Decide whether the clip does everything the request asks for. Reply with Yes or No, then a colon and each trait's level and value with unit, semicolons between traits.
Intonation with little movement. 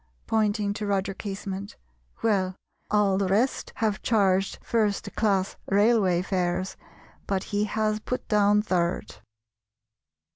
Yes: narrow, 1.9 semitones